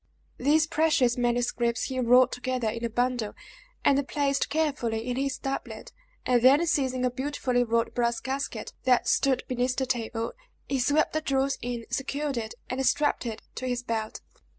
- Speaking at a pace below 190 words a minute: Yes, average, 170 wpm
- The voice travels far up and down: No, narrow, 2.4 semitones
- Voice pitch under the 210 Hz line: No, very high, 255 Hz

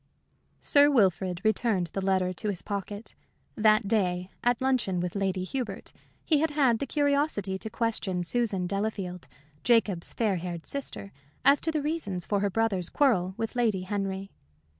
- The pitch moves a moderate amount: Yes, average, 4.7 semitones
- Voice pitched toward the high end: Yes, high, 205 Hz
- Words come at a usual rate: Yes, average, 160 wpm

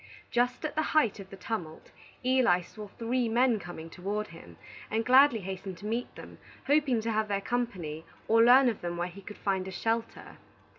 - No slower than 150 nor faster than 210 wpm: Yes, average, 195 wpm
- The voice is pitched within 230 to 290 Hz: No, high, 220 Hz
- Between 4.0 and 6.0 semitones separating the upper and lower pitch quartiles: Yes, average, 4.5 semitones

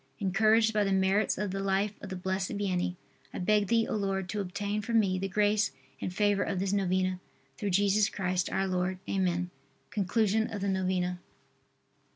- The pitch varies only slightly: Yes, narrow, 1.9 semitones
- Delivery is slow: No, average, 185 wpm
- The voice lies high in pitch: Yes, high, 195 Hz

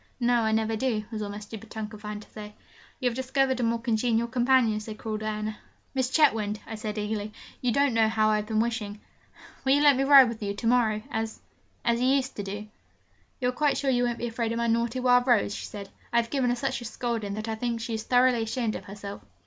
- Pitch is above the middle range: Yes, high, 230 Hz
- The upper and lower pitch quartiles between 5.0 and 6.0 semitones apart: No, narrow, 2.5 semitones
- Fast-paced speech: Yes, fast, 255 wpm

